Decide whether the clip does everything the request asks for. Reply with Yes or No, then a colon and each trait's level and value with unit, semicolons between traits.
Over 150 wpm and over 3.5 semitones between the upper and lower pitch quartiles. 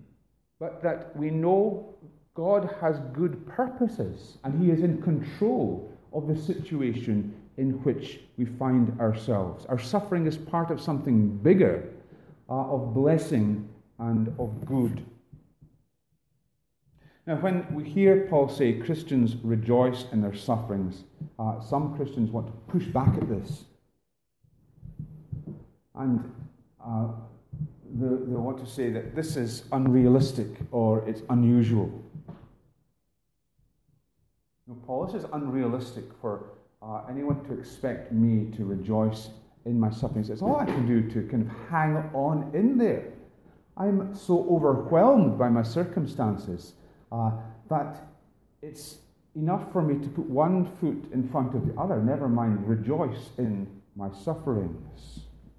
No: slow, 135 wpm; average, 5.3 semitones